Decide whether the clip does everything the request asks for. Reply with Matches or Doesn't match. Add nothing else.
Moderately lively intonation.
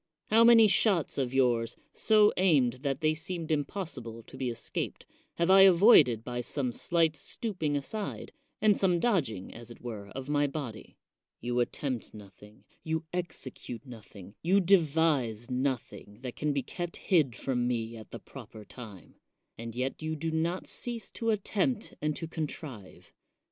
Doesn't match